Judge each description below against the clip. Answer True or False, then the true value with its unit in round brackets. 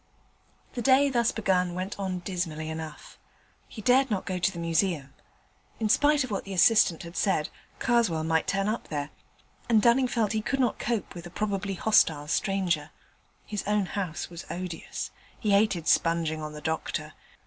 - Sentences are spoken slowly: False (175 wpm)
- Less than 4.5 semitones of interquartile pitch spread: False (4.8 semitones)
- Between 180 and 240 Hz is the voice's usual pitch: True (190 Hz)